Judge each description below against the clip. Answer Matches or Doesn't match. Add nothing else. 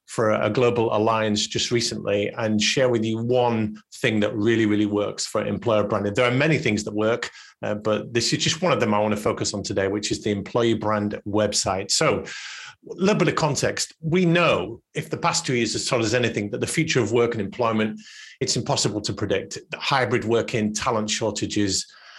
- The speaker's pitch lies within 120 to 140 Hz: Doesn't match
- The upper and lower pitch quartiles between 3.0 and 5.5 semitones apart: Doesn't match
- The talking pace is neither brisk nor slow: Doesn't match